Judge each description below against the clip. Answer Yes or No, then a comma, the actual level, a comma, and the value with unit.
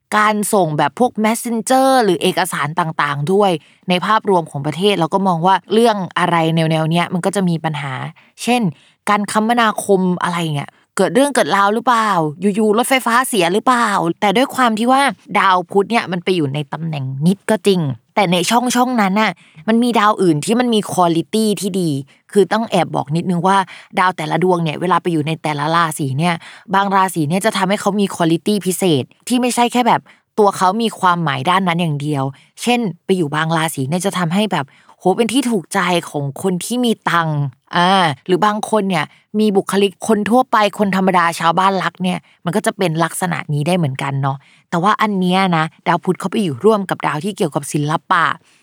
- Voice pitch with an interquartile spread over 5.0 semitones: No, average, 4.3 semitones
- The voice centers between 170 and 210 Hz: Yes, medium, 185 Hz